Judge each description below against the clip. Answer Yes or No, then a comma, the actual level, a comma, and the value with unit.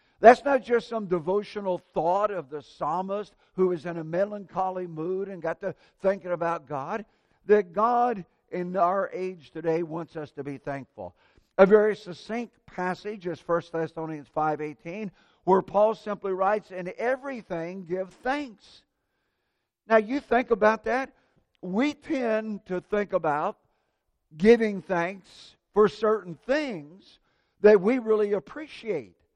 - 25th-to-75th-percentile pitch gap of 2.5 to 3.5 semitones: No, average, 4.0 semitones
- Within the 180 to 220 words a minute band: No, slow, 135 wpm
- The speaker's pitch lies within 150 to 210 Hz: Yes, high, 190 Hz